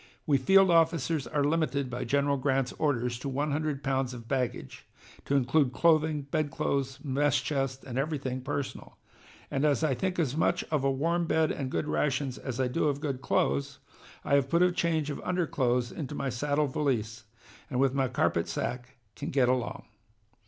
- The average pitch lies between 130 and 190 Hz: Yes, medium, 140 Hz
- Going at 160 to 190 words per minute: Yes, average, 180 wpm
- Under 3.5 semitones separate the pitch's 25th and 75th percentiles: Yes, average, 2.8 semitones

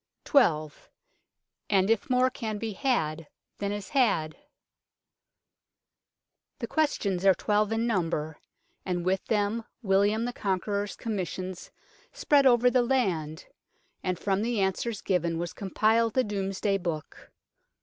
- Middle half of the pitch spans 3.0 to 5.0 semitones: Yes, average, 4.0 semitones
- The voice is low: No, high, 200 Hz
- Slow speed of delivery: Yes, slow, 125 wpm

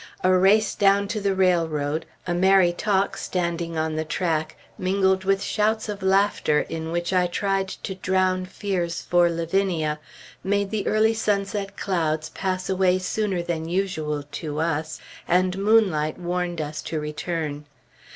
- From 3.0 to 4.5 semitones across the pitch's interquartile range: Yes, average, 3.3 semitones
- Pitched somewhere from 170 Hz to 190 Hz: Yes, medium, 185 Hz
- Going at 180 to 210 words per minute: No, average, 150 wpm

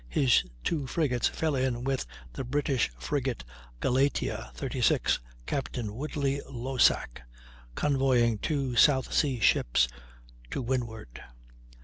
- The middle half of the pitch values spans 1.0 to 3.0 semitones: Yes, average, 2.7 semitones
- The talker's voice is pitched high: No, low, 130 Hz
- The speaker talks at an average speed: No, slow, 105 wpm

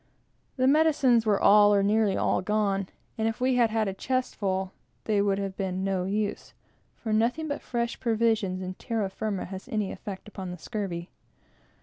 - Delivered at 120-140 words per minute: No, average, 190 wpm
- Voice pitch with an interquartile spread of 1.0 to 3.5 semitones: Yes, average, 2.9 semitones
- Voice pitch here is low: No, high, 210 Hz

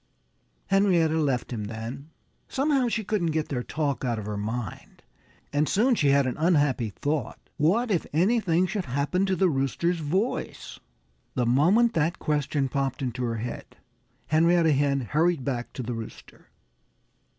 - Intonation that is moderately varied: No, wide, 5.8 semitones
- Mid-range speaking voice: Yes, medium, 150 Hz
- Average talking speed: Yes, average, 155 wpm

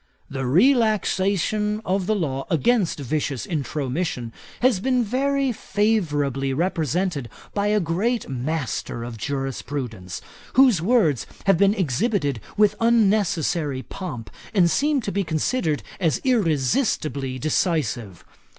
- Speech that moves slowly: Yes, slow, 115 wpm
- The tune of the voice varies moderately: No, wide, 7.4 semitones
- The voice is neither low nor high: Yes, medium, 170 Hz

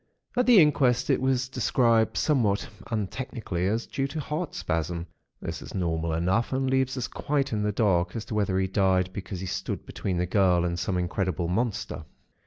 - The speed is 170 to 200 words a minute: Yes, average, 190 wpm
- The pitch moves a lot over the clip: Yes, wide, 6.3 semitones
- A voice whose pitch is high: No, low, 105 Hz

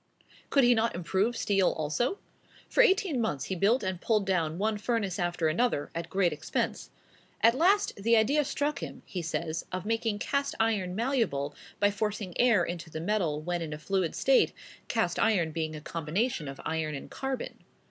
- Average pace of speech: Yes, average, 180 wpm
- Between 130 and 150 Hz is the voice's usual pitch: No, high, 195 Hz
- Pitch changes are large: Yes, wide, 5.8 semitones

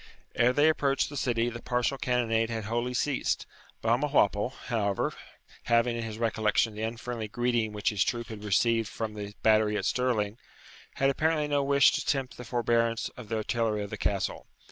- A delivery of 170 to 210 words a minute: Yes, average, 180 wpm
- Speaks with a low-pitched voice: Yes, low, 115 Hz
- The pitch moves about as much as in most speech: No, narrow, 2.3 semitones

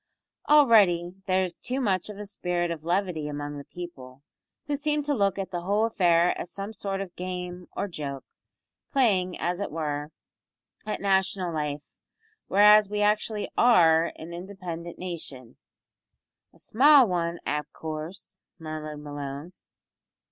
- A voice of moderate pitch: Yes, medium, 180 Hz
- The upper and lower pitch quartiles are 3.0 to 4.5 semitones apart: Yes, average, 4.1 semitones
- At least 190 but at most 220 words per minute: No, average, 150 wpm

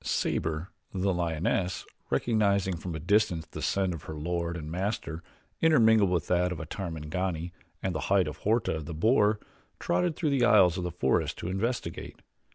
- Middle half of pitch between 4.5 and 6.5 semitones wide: No, average, 4.0 semitones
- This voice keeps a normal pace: Yes, average, 170 wpm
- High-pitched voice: No, very low, 90 Hz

